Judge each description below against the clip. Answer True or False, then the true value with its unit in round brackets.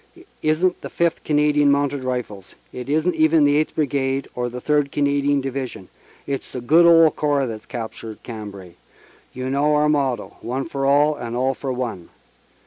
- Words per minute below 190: False (195 wpm)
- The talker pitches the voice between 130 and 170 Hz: True (140 Hz)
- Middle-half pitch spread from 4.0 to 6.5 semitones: False (3.2 semitones)